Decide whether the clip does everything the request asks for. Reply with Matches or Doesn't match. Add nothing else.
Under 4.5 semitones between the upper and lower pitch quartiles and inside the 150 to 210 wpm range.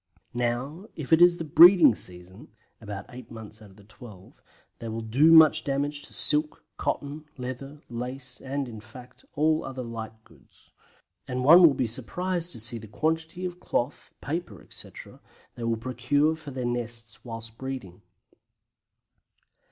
Doesn't match